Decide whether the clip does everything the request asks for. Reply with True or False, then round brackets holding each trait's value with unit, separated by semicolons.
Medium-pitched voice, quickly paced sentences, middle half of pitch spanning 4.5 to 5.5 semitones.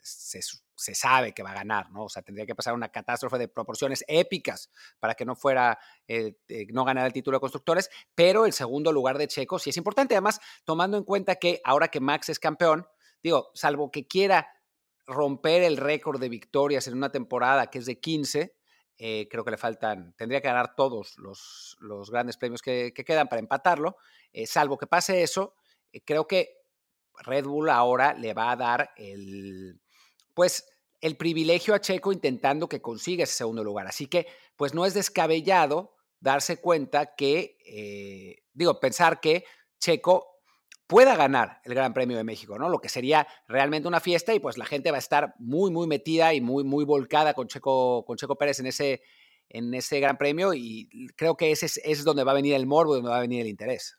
True (145 Hz; 200 wpm; 4.8 semitones)